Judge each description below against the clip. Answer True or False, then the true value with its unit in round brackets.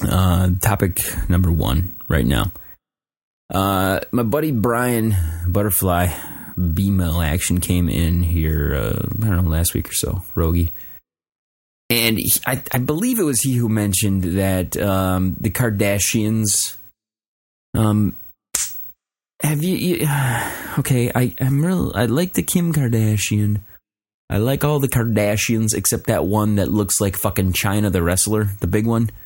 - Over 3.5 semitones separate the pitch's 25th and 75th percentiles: True (4.2 semitones)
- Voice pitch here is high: False (105 Hz)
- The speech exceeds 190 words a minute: False (145 wpm)